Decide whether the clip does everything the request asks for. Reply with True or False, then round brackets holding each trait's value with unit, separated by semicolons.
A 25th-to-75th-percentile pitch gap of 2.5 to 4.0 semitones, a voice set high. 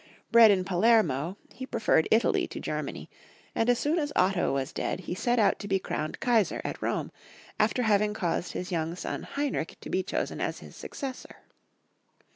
False (4.9 semitones; 200 Hz)